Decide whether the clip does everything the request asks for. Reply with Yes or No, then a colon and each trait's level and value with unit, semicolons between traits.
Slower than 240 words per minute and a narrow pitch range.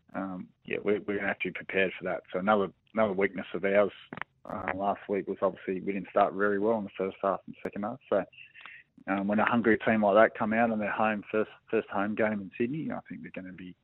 No: fast, 250 wpm; narrow, 2.0 semitones